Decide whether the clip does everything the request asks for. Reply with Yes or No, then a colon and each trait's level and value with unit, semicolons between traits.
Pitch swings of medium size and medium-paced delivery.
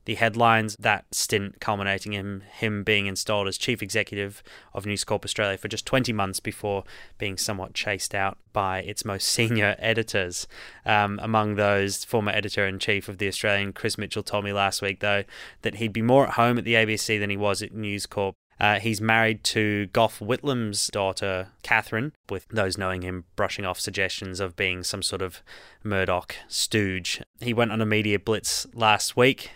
No: narrow, 2.0 semitones; average, 185 wpm